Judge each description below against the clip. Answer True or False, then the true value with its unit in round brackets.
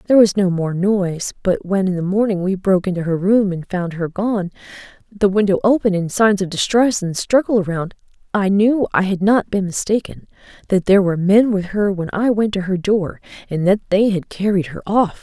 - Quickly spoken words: True (215 wpm)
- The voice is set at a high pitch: True (195 Hz)